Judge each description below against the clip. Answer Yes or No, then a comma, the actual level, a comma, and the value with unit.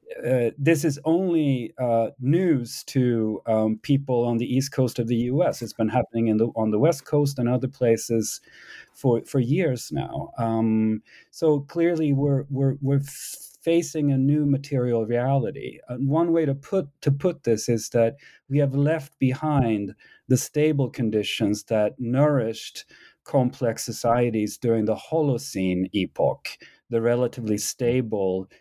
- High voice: No, low, 125 Hz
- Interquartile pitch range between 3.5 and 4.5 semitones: Yes, average, 3.8 semitones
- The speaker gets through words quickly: No, average, 150 wpm